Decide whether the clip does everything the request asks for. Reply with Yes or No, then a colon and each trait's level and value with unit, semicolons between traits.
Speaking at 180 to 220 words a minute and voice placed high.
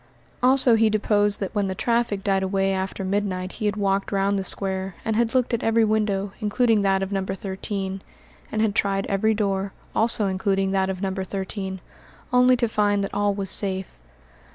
Yes: average, 190 wpm; high, 200 Hz